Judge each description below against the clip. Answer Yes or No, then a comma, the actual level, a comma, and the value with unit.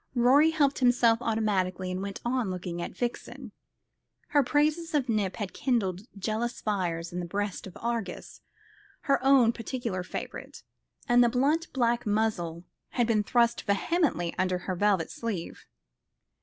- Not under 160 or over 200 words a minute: No, average, 145 wpm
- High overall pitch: Yes, high, 225 Hz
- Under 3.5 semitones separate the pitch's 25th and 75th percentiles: No, average, 4.9 semitones